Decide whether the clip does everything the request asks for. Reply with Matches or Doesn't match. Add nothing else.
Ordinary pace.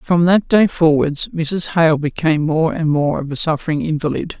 Matches